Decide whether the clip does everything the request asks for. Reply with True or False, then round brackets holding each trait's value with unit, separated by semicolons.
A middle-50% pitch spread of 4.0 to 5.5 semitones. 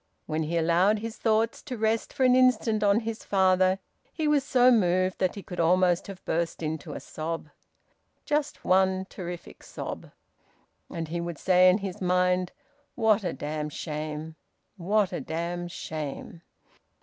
True (4.4 semitones)